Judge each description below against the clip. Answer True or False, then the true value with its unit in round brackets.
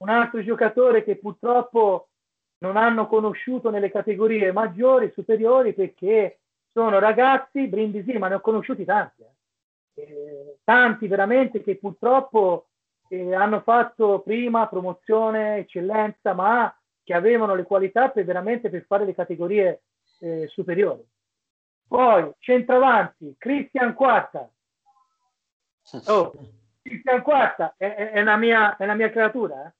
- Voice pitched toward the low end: False (220 Hz)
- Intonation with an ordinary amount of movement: True (4.0 semitones)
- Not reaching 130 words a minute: True (120 wpm)